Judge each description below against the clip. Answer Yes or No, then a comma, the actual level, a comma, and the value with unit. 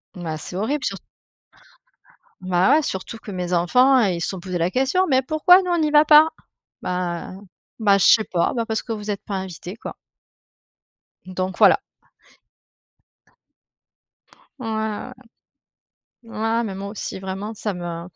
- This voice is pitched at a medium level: No, high, 205 Hz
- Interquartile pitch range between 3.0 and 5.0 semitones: No, wide, 5.6 semitones